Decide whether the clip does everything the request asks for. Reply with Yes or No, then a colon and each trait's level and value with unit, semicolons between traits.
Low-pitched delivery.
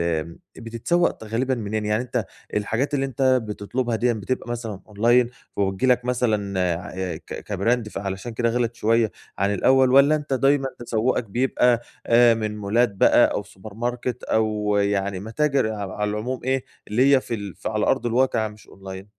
Yes: low, 115 Hz